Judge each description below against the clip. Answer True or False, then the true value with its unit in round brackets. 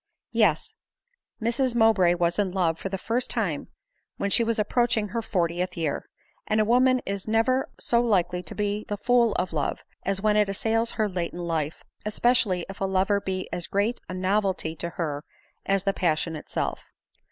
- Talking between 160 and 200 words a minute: True (185 wpm)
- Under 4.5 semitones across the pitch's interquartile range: True (4.0 semitones)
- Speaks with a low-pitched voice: False (195 Hz)